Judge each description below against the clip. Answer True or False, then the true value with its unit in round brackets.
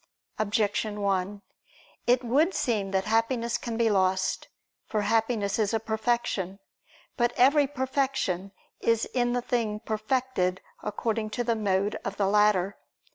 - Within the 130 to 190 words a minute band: True (135 wpm)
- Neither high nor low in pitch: False (220 Hz)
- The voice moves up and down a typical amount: True (3.2 semitones)